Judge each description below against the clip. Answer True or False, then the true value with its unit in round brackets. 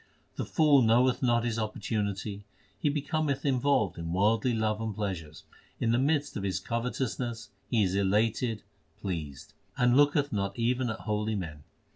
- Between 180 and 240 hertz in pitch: False (115 Hz)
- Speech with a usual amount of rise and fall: True (4.0 semitones)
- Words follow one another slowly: False (155 wpm)